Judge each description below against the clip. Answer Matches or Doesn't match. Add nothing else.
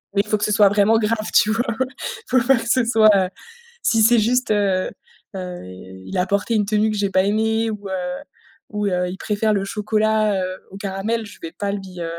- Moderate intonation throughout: Doesn't match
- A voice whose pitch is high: Matches